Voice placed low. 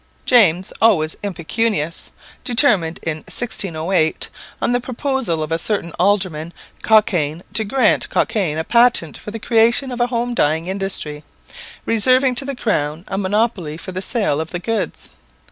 No: high, 195 Hz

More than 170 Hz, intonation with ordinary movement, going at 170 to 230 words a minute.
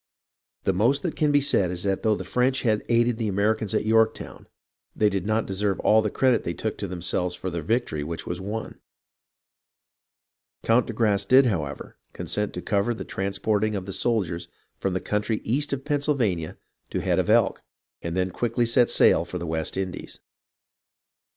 No: low, 105 Hz; average, 4.0 semitones; average, 190 wpm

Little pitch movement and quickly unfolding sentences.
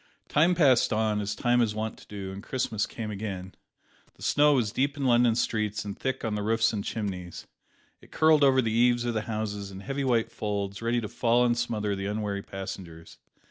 No: average, 3.1 semitones; fast, 210 wpm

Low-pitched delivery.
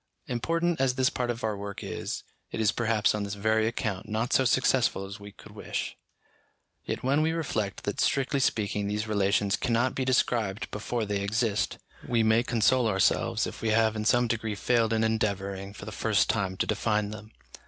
Yes: low, 110 Hz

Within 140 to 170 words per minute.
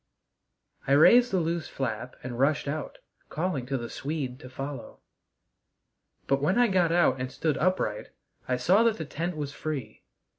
Yes: average, 165 wpm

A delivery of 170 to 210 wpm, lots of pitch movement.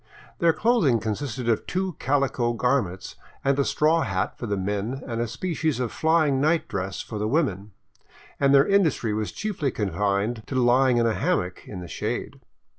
Yes: average, 180 wpm; wide, 6.2 semitones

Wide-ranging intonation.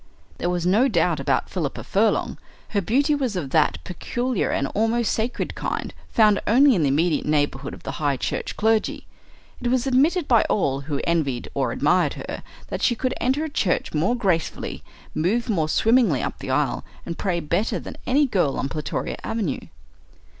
Yes: wide, 7.7 semitones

